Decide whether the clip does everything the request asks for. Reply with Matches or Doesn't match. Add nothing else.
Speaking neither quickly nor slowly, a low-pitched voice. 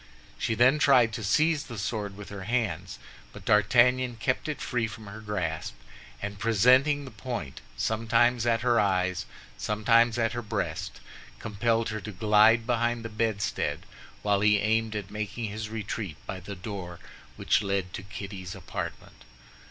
Matches